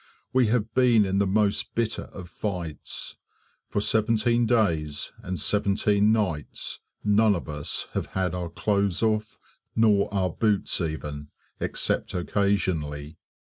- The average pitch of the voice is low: Yes, low, 100 Hz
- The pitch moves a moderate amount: Yes, average, 3.8 semitones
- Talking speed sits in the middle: No, slow, 130 wpm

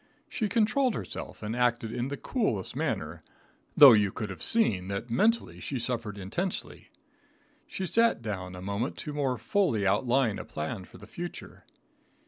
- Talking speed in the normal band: Yes, average, 160 wpm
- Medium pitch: No, low, 120 Hz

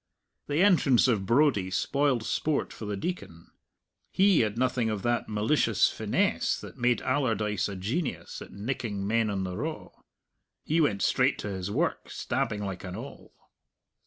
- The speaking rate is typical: Yes, average, 160 wpm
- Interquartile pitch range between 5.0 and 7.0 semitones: Yes, wide, 5.4 semitones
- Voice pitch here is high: No, low, 115 Hz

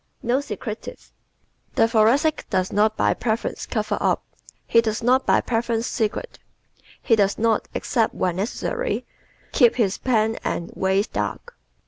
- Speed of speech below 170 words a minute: Yes, average, 145 wpm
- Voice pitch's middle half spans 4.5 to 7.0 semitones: No, average, 2.7 semitones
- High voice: Yes, high, 225 Hz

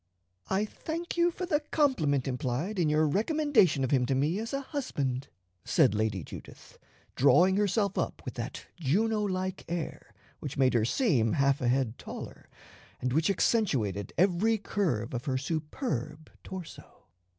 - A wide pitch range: Yes, wide, 8.3 semitones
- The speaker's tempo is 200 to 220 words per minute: No, average, 155 wpm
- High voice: No, medium, 160 Hz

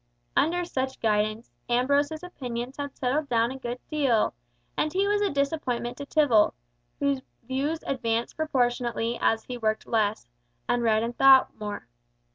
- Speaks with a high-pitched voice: Yes, very high, 255 Hz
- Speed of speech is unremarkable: Yes, average, 150 wpm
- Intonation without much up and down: No, average, 3.7 semitones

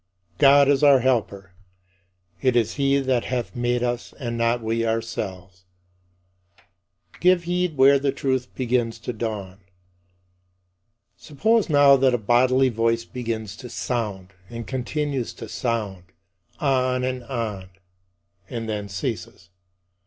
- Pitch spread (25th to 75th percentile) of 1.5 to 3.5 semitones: Yes, average, 3.2 semitones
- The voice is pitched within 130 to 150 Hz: No, low, 120 Hz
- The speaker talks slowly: Yes, slow, 125 wpm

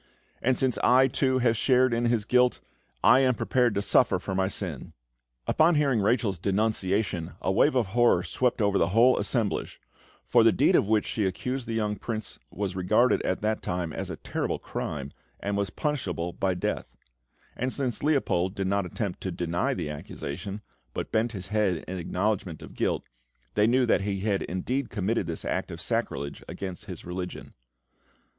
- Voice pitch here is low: Yes, low, 105 Hz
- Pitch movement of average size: Yes, average, 4.6 semitones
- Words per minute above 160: Yes, average, 180 wpm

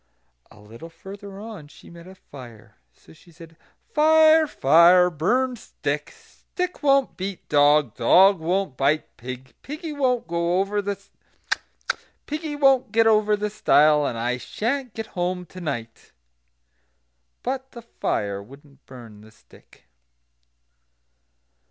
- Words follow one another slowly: Yes, slow, 120 wpm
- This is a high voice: No, medium, 180 Hz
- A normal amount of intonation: No, wide, 8.6 semitones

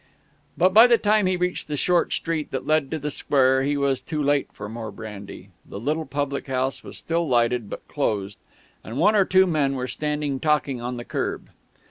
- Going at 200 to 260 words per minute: Yes, fast, 205 wpm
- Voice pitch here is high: No, medium, 145 Hz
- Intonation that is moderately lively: Yes, average, 4.3 semitones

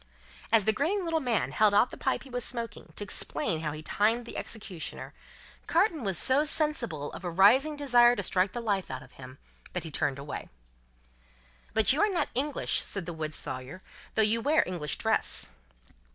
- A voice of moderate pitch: No, high, 215 Hz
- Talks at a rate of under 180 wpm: No, average, 195 wpm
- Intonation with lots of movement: Yes, wide, 7.6 semitones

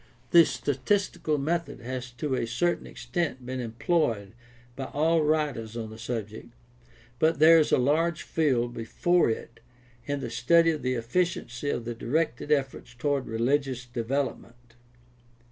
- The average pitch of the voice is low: Yes, low, 130 Hz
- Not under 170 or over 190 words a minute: No, average, 145 wpm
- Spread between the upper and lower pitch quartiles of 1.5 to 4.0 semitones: No, average, 4.8 semitones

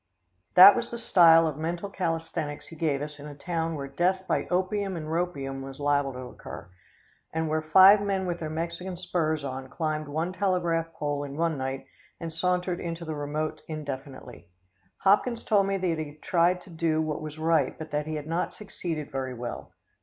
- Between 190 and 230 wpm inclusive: Yes, average, 195 wpm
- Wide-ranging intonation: No, average, 3.3 semitones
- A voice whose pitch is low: No, medium, 160 Hz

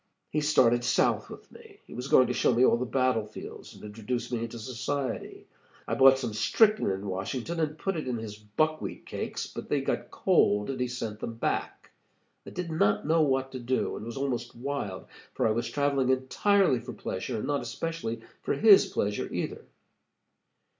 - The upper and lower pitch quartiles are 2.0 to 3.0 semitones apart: No, average, 3.9 semitones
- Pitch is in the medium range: No, low, 125 Hz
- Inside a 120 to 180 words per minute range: No, average, 195 wpm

